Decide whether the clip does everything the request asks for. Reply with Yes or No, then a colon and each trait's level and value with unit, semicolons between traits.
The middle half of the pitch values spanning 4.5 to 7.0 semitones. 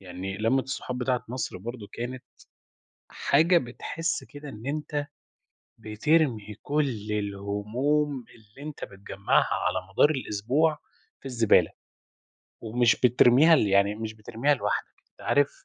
Yes: average, 5.2 semitones